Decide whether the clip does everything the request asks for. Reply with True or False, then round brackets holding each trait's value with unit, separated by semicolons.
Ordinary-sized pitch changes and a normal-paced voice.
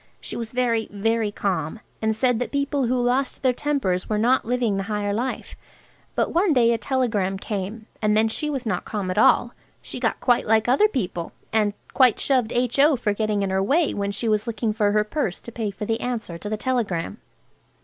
False (3.3 semitones; 210 wpm)